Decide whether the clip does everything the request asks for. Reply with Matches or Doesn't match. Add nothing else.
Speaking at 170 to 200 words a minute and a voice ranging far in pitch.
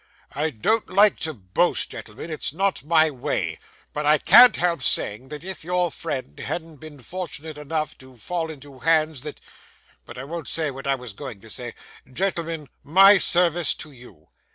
Doesn't match